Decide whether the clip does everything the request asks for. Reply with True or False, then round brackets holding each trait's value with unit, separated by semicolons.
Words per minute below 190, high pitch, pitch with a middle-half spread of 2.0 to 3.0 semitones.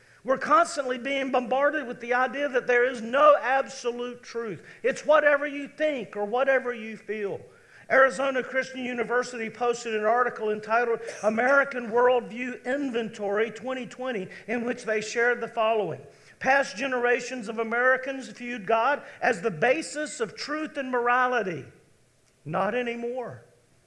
True (135 wpm; 245 Hz; 2.6 semitones)